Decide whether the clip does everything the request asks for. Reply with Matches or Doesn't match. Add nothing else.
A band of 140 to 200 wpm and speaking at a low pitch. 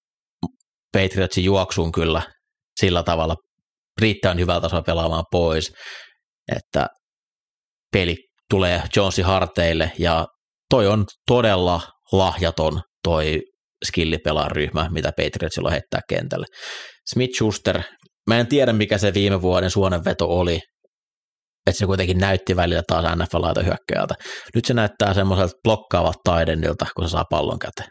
Doesn't match